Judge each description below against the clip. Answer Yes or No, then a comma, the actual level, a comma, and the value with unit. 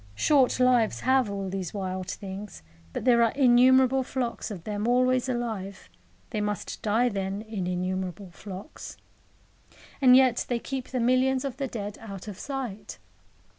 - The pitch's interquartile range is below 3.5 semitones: No, average, 4.5 semitones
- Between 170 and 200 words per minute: No, average, 155 wpm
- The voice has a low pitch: No, high, 225 Hz